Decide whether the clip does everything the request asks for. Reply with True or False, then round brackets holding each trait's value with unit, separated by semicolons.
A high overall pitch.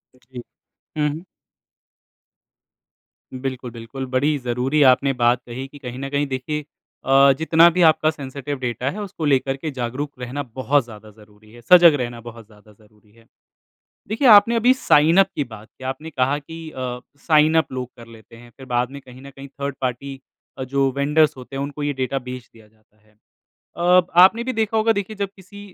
False (135 Hz)